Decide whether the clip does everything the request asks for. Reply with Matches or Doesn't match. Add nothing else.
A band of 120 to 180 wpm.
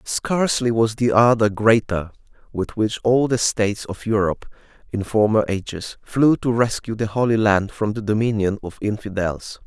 Matches